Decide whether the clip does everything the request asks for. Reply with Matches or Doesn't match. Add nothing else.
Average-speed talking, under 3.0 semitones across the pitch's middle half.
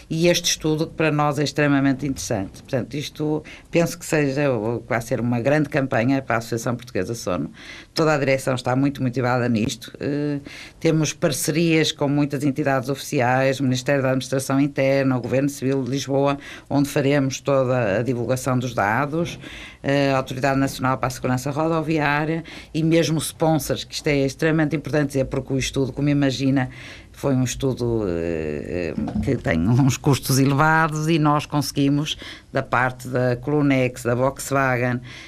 Matches